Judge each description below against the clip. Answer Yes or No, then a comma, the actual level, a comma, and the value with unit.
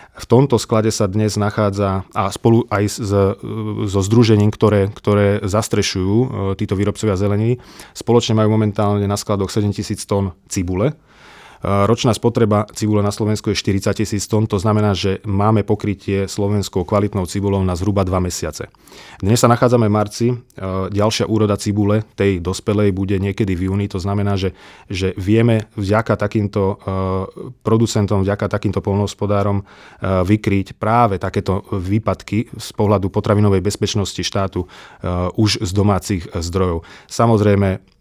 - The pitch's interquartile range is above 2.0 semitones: No, narrow, 1.7 semitones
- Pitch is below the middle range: Yes, low, 105 Hz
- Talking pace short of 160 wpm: Yes, average, 135 wpm